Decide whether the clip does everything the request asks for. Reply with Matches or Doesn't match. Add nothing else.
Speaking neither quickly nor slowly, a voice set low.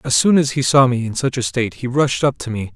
Doesn't match